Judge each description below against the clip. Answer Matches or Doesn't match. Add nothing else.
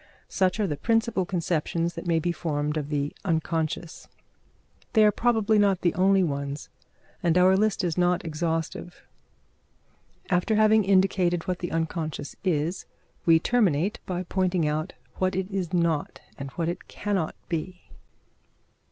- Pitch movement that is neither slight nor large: Matches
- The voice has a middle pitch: Matches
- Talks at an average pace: Matches